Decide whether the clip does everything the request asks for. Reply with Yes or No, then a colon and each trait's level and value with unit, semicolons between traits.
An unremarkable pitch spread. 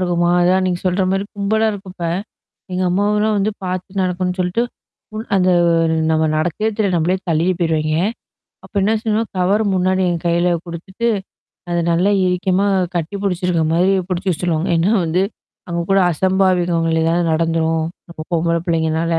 No: narrow, 2.2 semitones